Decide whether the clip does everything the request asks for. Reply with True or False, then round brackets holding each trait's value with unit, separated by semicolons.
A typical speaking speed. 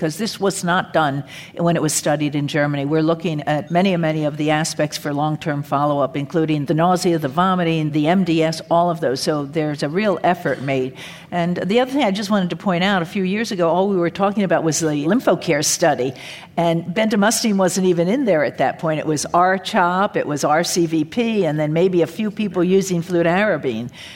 False (215 wpm)